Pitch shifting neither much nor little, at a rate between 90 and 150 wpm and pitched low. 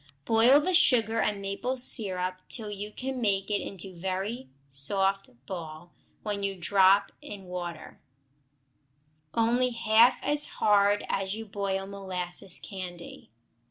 No: average, 3.1 semitones; slow, 135 wpm; high, 200 Hz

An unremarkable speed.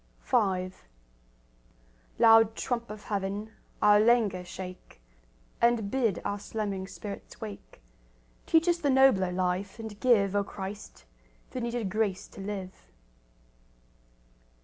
No: slow, 115 wpm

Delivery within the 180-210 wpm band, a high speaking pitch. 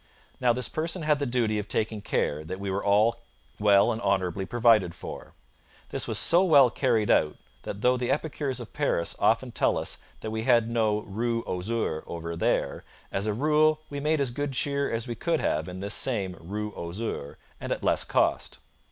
No: fast, 205 wpm; low, 115 Hz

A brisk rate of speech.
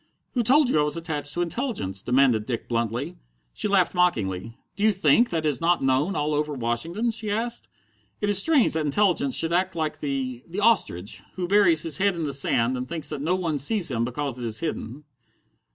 Yes: fast, 210 wpm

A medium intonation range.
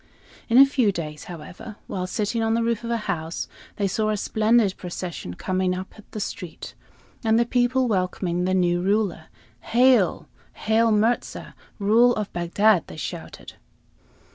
Yes: average, 4.1 semitones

